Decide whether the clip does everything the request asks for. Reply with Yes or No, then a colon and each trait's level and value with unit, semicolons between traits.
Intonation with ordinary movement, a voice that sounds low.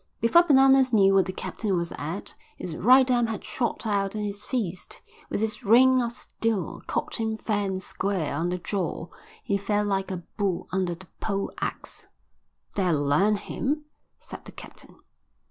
No: average, 3.5 semitones; high, 205 Hz